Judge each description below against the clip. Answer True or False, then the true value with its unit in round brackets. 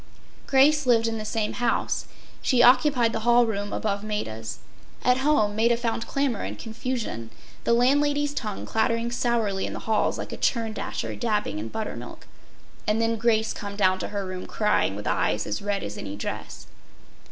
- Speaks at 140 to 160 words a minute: False (175 wpm)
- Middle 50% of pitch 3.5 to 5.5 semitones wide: False (3.0 semitones)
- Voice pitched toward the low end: False (225 Hz)